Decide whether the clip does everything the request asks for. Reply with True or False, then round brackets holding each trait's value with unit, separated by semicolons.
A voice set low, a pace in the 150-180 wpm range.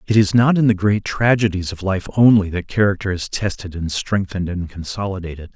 False (95 Hz; 195 wpm)